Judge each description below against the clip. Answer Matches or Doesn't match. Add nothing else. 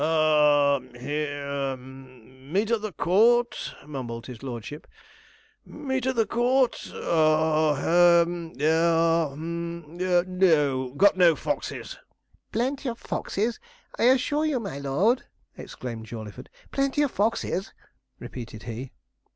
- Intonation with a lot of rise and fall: Matches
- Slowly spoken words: Matches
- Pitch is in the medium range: Matches